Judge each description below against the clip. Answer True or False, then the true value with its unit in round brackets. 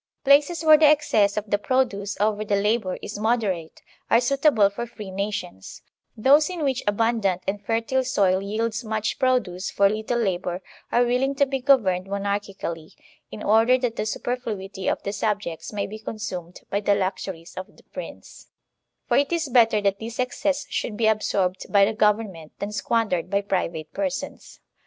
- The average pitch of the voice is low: False (210 Hz)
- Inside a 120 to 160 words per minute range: False (175 wpm)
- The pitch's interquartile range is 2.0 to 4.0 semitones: True (3.7 semitones)